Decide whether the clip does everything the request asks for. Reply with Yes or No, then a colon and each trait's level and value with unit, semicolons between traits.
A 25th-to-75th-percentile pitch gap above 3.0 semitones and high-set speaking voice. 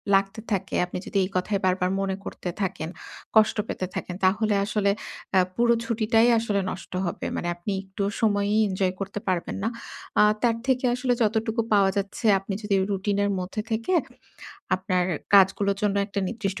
No: narrow, 2.5 semitones; high, 200 Hz